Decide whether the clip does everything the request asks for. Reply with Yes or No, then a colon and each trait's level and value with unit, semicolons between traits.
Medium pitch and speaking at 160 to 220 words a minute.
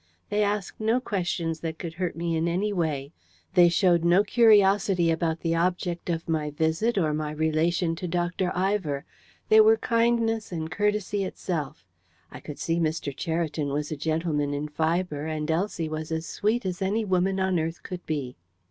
Yes: medium, 170 Hz; average, 175 wpm